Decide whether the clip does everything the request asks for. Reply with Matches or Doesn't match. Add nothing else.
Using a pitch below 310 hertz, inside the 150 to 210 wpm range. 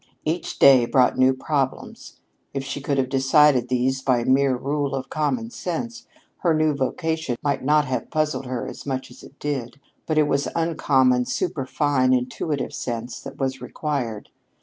Matches